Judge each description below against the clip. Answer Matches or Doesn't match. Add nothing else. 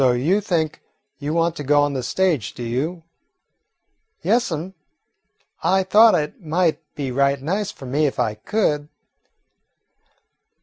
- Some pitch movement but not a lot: Matches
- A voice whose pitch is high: Doesn't match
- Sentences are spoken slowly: Doesn't match